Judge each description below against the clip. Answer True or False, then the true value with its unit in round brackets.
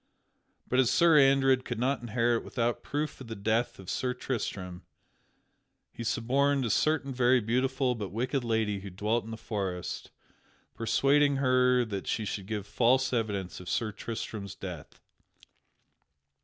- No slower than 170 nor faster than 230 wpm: False (150 wpm)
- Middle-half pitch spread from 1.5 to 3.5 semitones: False (3.9 semitones)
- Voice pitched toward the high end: False (120 Hz)